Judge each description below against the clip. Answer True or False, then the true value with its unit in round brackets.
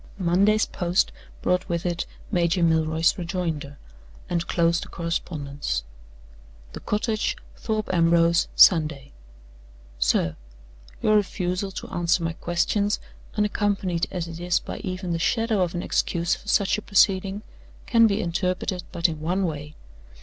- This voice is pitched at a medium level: True (175 Hz)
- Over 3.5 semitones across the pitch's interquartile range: False (2.7 semitones)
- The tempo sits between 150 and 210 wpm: False (135 wpm)